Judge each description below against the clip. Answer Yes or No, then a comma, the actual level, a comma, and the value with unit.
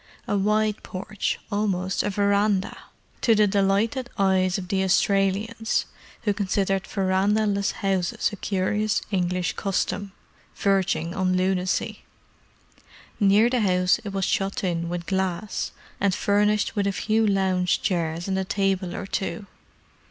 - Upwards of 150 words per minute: No, slow, 135 wpm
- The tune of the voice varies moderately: No, narrow, 1.7 semitones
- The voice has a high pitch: Yes, high, 195 Hz